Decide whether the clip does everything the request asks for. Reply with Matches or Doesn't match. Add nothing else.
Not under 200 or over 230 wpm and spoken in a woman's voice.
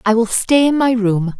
Doesn't match